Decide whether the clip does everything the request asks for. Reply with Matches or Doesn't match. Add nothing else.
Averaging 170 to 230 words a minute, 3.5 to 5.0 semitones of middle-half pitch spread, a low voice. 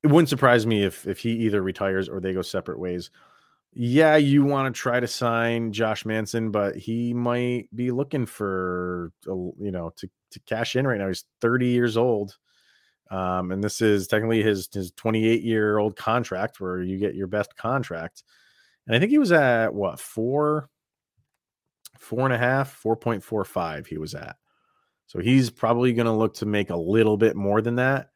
Matches